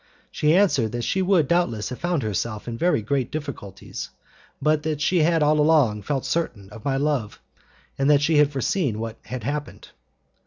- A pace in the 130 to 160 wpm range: No, average, 185 wpm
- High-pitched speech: No, medium, 145 Hz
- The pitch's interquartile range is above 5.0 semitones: Yes, wide, 5.4 semitones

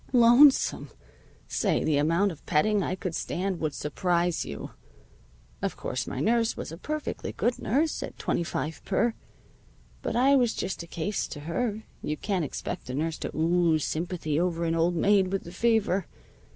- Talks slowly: No, average, 175 wpm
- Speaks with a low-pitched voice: No, medium, 180 Hz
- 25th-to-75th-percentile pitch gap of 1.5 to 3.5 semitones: No, average, 5.1 semitones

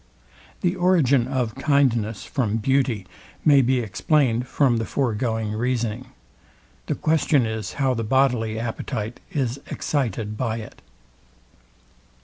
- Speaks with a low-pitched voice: Yes, low, 125 Hz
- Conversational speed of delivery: No, slow, 120 wpm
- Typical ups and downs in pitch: Yes, average, 3.5 semitones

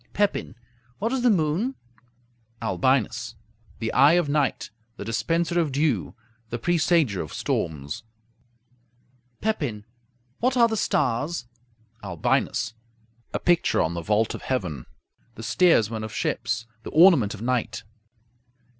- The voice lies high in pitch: No, low, 130 Hz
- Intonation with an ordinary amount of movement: No, wide, 7.9 semitones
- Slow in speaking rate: Yes, slow, 125 wpm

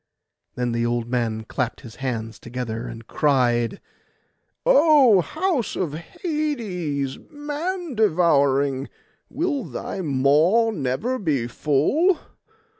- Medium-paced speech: No, slow, 105 wpm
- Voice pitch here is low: No, medium, 150 Hz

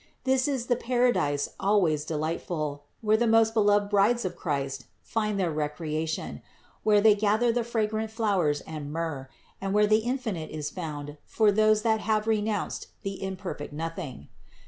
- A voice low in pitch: No, high, 205 Hz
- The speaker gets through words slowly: No, average, 155 wpm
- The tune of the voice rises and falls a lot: Yes, wide, 5.9 semitones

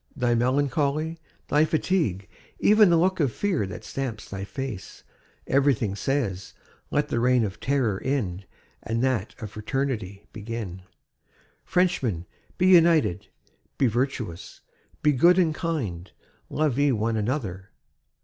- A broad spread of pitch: Yes, wide, 6.4 semitones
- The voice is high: No, low, 125 Hz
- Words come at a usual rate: No, slow, 130 wpm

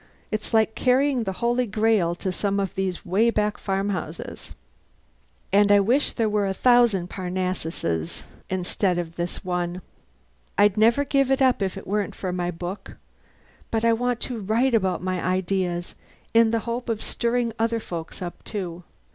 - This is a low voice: No, high, 200 Hz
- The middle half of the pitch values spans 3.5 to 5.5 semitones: Yes, average, 4.1 semitones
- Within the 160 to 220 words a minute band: Yes, average, 165 wpm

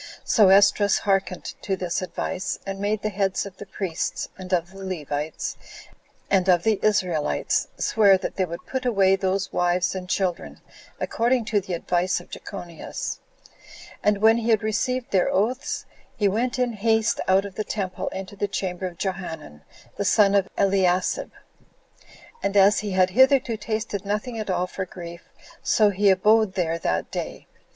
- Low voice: No, high, 195 Hz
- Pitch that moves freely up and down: No, narrow, 2.6 semitones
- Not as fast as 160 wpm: No, average, 170 wpm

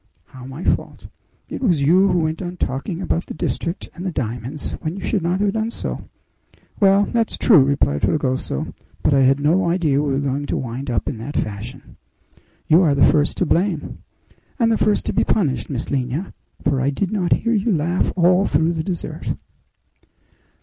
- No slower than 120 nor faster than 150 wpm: No, average, 195 wpm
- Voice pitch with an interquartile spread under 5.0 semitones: No, wide, 5.5 semitones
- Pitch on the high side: No, medium, 160 Hz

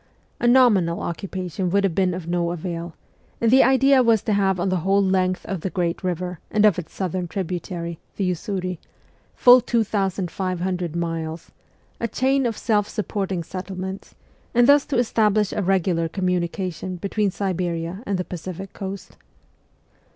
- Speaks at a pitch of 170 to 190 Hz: Yes, medium, 185 Hz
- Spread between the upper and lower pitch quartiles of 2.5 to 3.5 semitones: Yes, average, 2.8 semitones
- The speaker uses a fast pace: No, average, 160 wpm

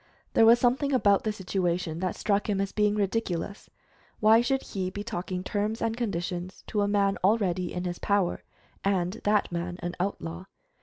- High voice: Yes, high, 200 Hz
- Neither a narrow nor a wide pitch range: Yes, average, 3.0 semitones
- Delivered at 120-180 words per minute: Yes, average, 175 wpm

